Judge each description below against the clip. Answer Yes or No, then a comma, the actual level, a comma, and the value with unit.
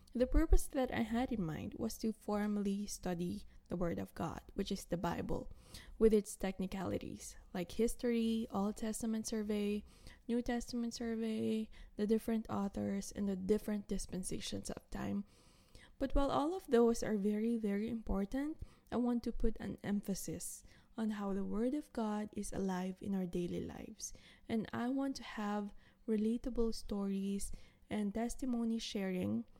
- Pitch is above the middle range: Yes, high, 215 Hz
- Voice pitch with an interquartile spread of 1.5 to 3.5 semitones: Yes, average, 2.8 semitones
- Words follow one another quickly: No, average, 155 wpm